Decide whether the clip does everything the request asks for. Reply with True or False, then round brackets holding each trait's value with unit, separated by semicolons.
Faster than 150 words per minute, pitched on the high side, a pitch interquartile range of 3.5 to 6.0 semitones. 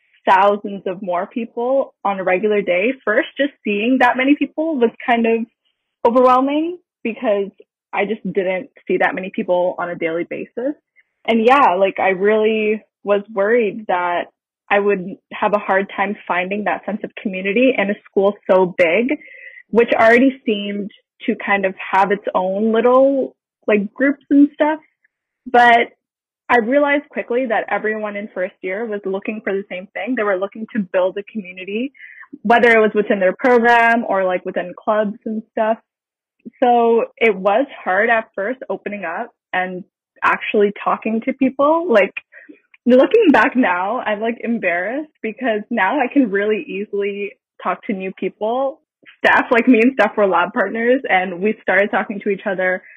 True (165 wpm; 220 Hz; 3.9 semitones)